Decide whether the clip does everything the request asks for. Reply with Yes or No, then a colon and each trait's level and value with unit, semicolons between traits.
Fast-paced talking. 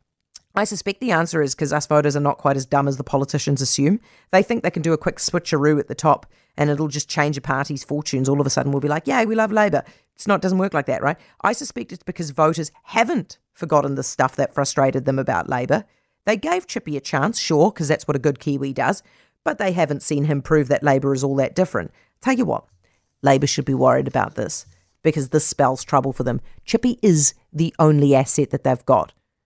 Yes: fast, 235 wpm